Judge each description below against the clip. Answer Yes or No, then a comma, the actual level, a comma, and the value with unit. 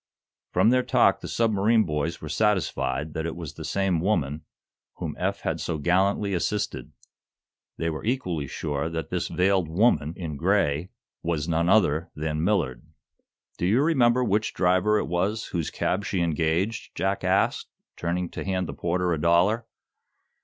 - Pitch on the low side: Yes, very low, 90 Hz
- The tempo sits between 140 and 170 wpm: Yes, average, 160 wpm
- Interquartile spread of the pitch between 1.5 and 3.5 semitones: No, average, 4.1 semitones